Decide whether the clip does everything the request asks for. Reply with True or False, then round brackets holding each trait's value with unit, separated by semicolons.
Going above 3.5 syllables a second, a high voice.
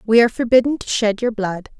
True (6.3 syllables/s; 225 Hz)